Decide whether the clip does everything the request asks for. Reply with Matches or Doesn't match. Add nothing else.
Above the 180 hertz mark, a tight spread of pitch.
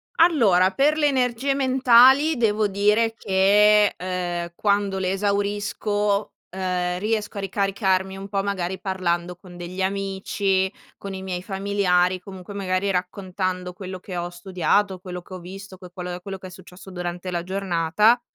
Matches